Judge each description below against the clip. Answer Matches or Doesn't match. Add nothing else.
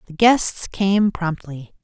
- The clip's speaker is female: Matches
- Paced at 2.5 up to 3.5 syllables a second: Matches